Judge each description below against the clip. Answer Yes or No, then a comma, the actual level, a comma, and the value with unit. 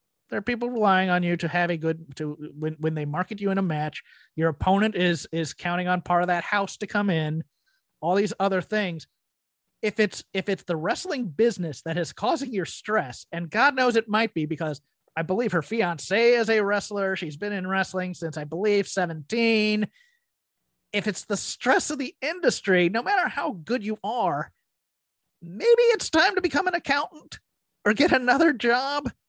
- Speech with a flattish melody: No, wide, 5.6 semitones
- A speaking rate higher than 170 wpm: Yes, average, 195 wpm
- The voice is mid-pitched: No, high, 195 Hz